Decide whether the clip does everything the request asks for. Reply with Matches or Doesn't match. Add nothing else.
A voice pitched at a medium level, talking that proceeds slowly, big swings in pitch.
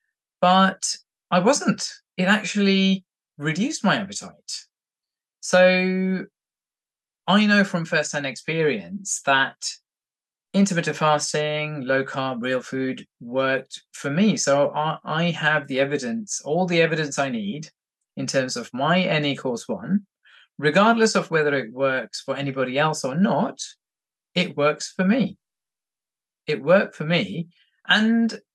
Matches